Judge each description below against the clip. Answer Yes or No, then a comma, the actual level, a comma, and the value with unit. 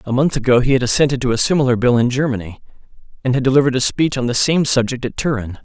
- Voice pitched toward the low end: Yes, low, 130 Hz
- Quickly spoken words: Yes, fast, 245 wpm